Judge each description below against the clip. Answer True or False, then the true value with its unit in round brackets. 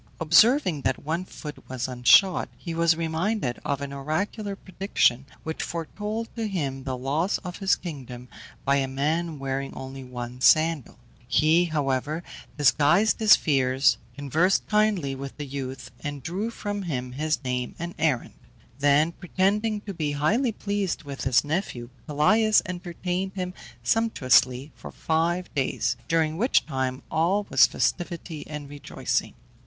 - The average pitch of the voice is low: False (155 Hz)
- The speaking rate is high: False (145 wpm)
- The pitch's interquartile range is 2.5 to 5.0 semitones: False (5.4 semitones)